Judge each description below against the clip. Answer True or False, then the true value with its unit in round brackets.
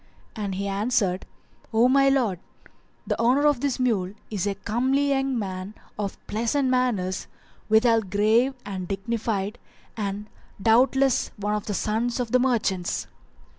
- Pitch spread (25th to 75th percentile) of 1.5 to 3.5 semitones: False (4.1 semitones)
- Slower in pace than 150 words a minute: True (140 wpm)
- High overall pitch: True (220 Hz)